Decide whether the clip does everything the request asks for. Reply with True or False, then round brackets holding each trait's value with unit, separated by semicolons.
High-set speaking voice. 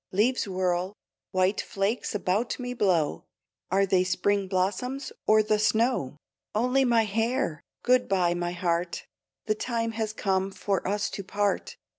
True (200 Hz)